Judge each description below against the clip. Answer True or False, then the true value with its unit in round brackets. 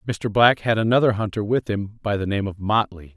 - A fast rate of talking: True (230 wpm)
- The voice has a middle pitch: False (105 Hz)